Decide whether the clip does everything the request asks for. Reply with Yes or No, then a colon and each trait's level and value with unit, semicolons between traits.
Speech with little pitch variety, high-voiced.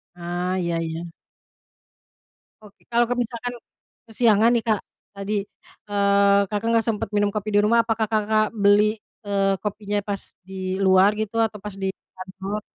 Yes: narrow, 1.9 semitones; high, 205 Hz